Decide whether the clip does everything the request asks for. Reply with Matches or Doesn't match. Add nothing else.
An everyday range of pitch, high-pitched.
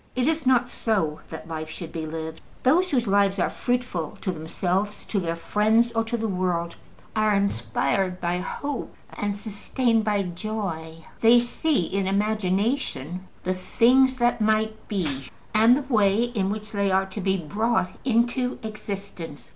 Matches